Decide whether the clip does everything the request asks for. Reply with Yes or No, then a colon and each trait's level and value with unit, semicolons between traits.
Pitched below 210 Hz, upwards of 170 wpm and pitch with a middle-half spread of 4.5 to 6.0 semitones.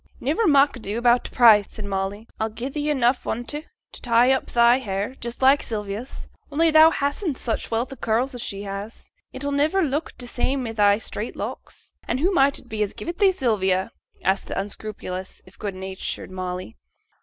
No: high, 235 Hz; average, 200 wpm; average, 5.2 semitones